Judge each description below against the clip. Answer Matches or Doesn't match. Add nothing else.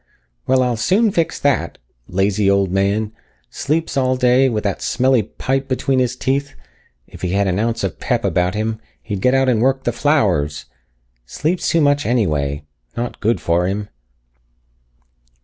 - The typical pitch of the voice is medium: Doesn't match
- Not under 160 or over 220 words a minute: Matches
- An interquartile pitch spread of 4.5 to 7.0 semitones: Matches